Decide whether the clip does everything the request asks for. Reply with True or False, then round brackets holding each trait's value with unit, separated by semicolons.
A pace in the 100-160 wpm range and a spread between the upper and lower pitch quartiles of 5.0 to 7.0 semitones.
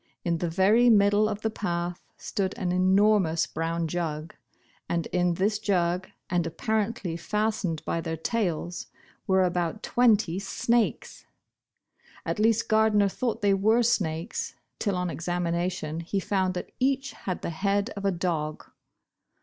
False (145 wpm; 3.8 semitones)